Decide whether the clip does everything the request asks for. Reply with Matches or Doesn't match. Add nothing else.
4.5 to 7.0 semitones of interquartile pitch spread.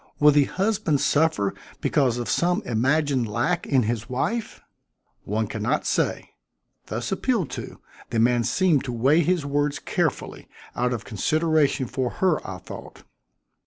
Matches